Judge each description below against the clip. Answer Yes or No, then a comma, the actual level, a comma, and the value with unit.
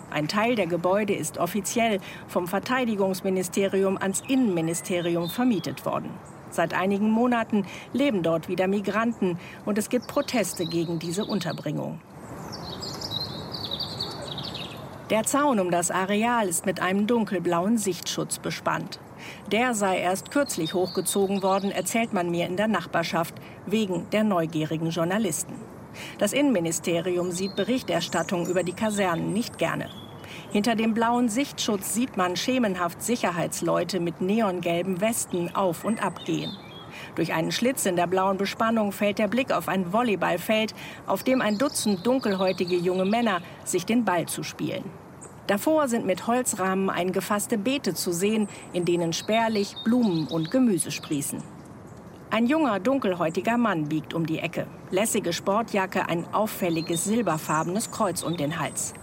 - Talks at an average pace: Yes, average, 135 wpm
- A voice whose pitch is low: No, high, 195 Hz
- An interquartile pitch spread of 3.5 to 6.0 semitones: Yes, average, 4.2 semitones